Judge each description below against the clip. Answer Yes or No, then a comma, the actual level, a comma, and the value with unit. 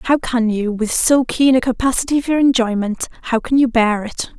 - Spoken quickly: No, average, 190 wpm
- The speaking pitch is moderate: No, high, 245 Hz